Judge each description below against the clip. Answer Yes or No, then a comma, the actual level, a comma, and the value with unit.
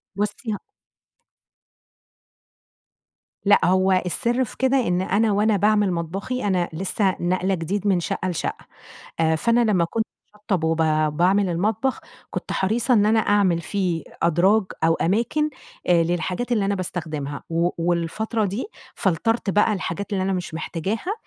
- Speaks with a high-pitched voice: Yes, high, 195 Hz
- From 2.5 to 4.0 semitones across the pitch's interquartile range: Yes, average, 3.7 semitones